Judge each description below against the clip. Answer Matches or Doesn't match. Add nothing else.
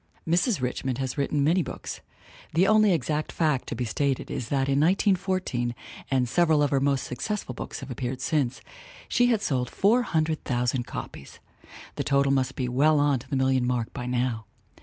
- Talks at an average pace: Matches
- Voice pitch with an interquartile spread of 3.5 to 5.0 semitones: Matches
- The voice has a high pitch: Doesn't match